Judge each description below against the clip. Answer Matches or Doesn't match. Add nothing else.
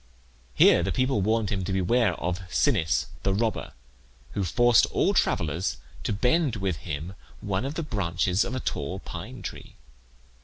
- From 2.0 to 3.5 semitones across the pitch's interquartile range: Doesn't match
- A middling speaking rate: Matches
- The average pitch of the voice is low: Matches